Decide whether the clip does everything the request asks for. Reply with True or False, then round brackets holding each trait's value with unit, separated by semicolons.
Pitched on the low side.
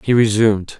True (110 Hz)